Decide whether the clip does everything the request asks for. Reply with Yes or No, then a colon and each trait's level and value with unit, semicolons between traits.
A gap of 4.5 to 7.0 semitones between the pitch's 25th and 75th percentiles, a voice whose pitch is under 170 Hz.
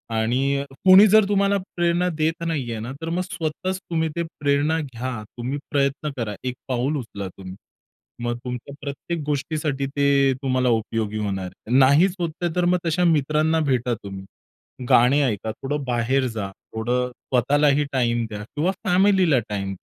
Yes: average, 5.2 semitones; medium, 140 Hz